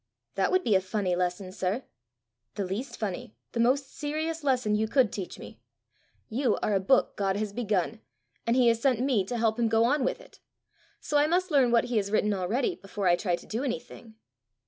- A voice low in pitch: No, high, 230 Hz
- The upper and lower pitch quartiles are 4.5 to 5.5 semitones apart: Yes, average, 4.8 semitones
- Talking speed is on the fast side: Yes, fast, 215 wpm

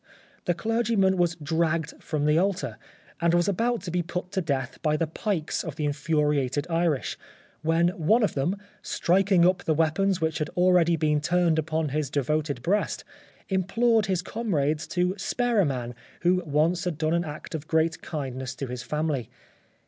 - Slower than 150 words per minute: No, average, 175 wpm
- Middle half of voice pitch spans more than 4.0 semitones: No, average, 3.2 semitones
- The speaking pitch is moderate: Yes, medium, 165 Hz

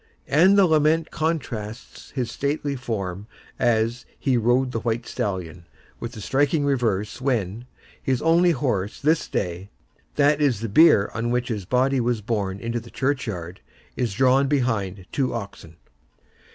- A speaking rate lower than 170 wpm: Yes, average, 140 wpm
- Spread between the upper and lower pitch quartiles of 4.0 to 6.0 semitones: Yes, average, 5.1 semitones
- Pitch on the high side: No, low, 120 Hz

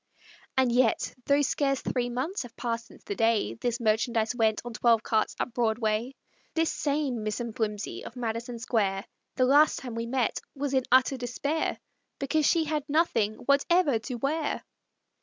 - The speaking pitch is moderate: No, high, 245 Hz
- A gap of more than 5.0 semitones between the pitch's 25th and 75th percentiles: No, average, 3.7 semitones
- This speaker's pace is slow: No, average, 165 wpm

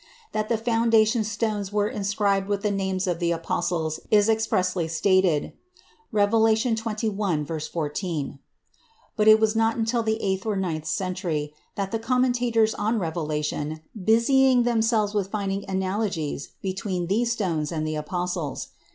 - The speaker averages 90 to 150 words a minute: Yes, average, 140 wpm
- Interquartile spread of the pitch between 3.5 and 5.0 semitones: Yes, average, 4.3 semitones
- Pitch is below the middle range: No, high, 200 Hz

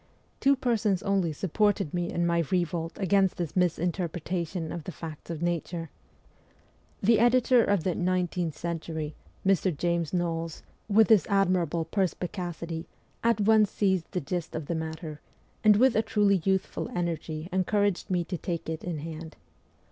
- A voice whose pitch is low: No, medium, 175 Hz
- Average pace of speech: Yes, average, 160 wpm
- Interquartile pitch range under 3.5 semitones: Yes, average, 3.1 semitones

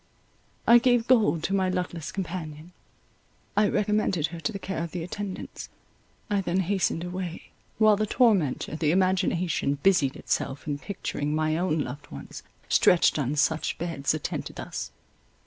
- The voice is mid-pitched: Yes, medium, 180 Hz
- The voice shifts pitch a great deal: No, average, 4.2 semitones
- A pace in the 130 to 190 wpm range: Yes, average, 150 wpm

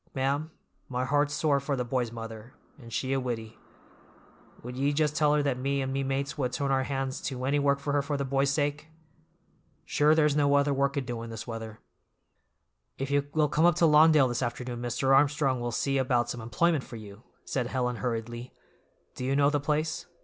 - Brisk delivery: Yes, fast, 210 wpm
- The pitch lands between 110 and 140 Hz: Yes, low, 135 Hz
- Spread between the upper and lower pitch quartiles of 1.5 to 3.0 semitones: Yes, average, 2.7 semitones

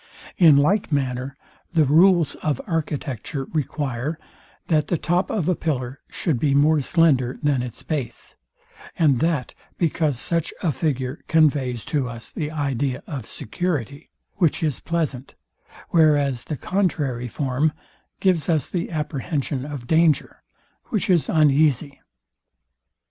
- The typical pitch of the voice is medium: Yes, medium, 150 Hz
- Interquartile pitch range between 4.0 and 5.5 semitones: No, average, 3.5 semitones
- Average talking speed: No, slow, 130 wpm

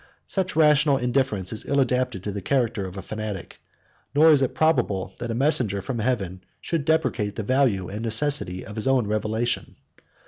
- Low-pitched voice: Yes, low, 120 Hz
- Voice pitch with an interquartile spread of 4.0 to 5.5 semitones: Yes, average, 5.1 semitones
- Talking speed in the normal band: Yes, average, 180 wpm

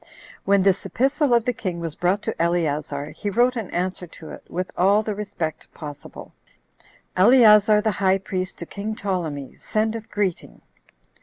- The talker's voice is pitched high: Yes, high, 195 Hz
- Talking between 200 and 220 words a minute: No, average, 165 wpm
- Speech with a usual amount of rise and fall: Yes, average, 3.7 semitones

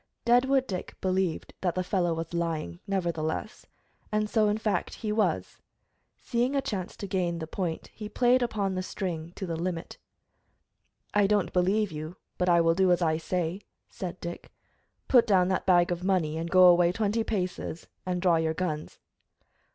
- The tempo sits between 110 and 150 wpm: No, average, 175 wpm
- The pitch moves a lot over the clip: No, average, 3.5 semitones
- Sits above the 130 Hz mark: Yes, medium, 185 Hz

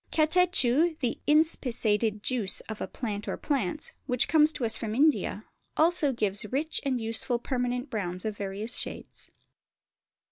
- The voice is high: Yes, high, 245 Hz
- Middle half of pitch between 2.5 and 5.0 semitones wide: No, wide, 5.6 semitones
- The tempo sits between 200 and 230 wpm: No, average, 145 wpm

